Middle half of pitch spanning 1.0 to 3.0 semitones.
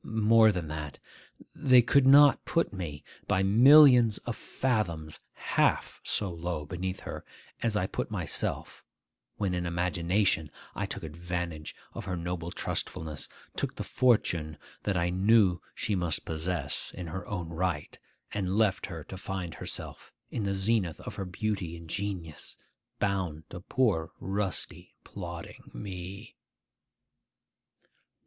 No: average, 3.7 semitones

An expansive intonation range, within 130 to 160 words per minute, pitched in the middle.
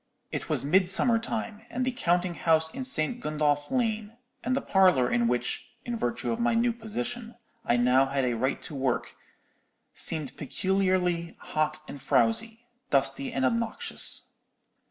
Yes: wide, 8.7 semitones; average, 145 wpm; medium, 180 Hz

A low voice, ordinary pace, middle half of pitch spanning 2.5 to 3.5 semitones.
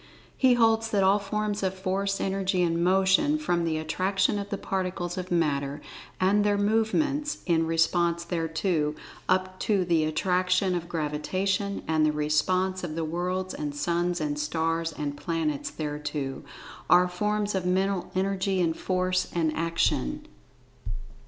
No: medium, 180 Hz; average, 145 wpm; average, 3.1 semitones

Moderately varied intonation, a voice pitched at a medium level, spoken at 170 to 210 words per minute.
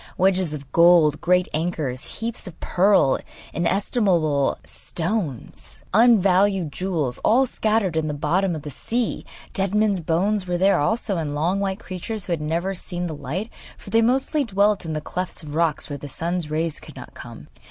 Yes: average, 4.3 semitones; medium, 180 Hz; average, 175 wpm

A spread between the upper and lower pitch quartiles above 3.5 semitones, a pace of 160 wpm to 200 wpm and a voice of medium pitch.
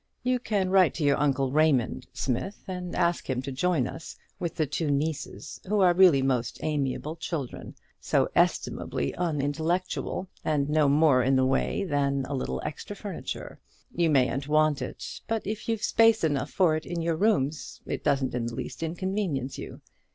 Yes: average, 4.7 semitones; average, 175 wpm; medium, 155 Hz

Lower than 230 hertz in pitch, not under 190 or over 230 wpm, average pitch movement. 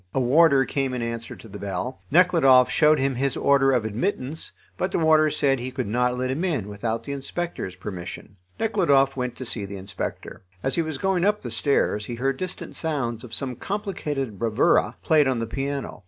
Yes: low, 135 Hz; average, 200 wpm; average, 4.6 semitones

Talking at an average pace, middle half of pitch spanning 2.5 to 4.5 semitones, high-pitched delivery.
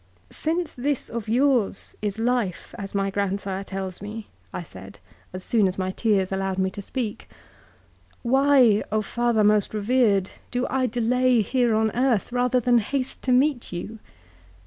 Yes: average, 170 wpm; average, 4.2 semitones; high, 220 Hz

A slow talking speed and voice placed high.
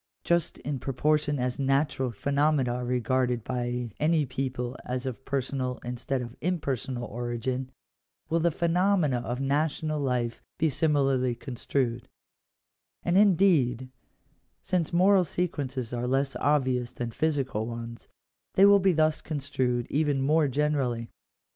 No: slow, 130 wpm; low, 135 Hz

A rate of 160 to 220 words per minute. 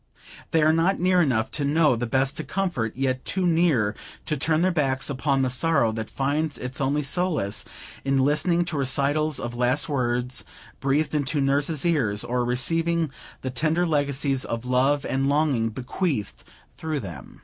Yes: average, 170 wpm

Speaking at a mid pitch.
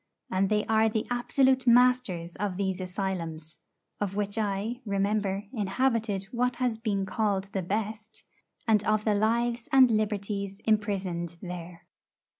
No: high, 210 Hz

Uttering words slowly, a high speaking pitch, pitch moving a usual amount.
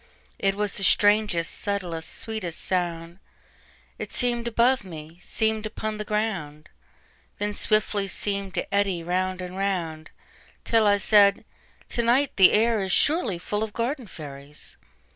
Yes: slow, 125 wpm; high, 200 Hz; average, 3.7 semitones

